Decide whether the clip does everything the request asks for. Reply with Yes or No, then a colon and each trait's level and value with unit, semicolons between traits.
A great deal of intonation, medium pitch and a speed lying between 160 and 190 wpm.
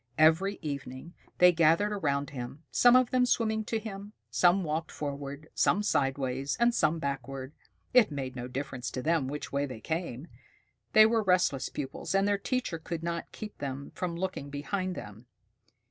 Yes: wide, 6.0 semitones; medium, 160 Hz; average, 170 wpm